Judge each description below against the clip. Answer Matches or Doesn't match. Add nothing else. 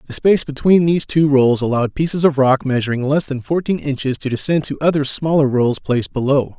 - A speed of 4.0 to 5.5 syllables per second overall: Doesn't match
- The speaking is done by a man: Matches